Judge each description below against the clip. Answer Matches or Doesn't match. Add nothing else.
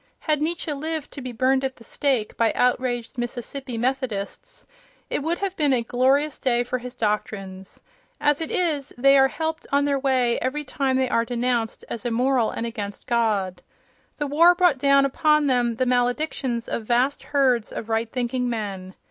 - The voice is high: Matches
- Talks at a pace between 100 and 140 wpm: Doesn't match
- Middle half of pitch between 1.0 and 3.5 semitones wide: Matches